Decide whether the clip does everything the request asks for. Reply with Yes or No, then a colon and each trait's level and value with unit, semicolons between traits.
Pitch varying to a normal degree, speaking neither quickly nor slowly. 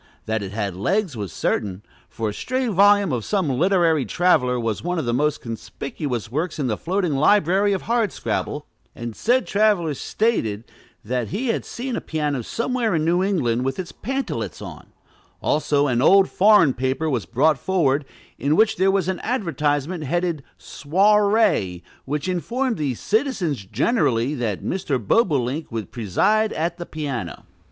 No: wide, 8.0 semitones; average, 160 wpm